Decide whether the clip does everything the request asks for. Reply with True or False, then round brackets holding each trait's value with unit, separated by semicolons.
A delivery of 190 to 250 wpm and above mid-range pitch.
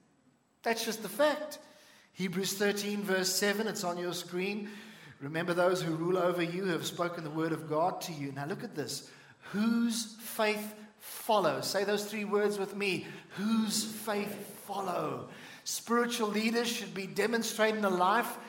False (160 wpm; 205 Hz)